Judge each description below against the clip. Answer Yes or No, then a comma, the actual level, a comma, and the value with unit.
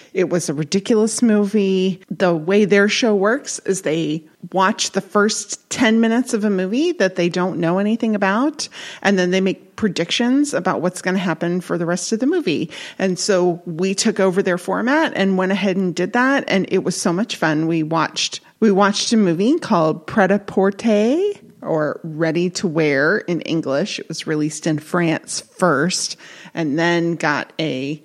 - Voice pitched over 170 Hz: Yes, high, 190 Hz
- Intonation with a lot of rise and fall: No, average, 3.8 semitones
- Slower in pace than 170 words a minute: No, average, 185 wpm